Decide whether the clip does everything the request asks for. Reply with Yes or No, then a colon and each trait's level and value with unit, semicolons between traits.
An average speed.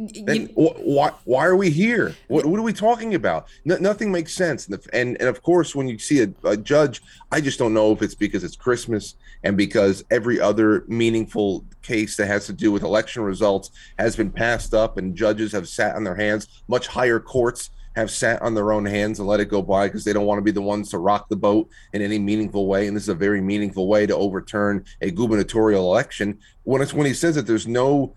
No: fast, 230 wpm